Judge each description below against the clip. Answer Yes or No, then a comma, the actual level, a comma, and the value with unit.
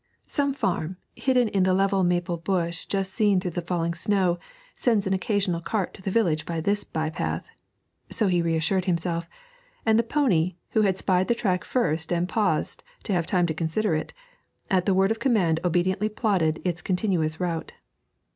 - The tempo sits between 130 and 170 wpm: No, average, 185 wpm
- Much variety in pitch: No, average, 3.3 semitones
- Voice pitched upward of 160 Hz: Yes, medium, 185 Hz